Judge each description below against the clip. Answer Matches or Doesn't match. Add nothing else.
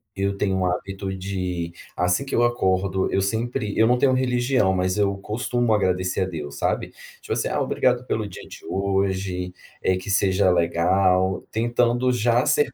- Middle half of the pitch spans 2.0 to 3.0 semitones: Doesn't match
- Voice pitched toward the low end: Matches